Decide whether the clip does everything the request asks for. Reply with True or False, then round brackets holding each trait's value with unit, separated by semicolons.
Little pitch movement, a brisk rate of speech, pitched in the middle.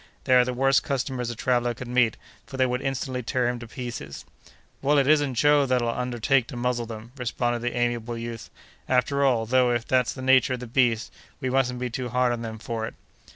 False (1.5 semitones; 220 wpm; 125 Hz)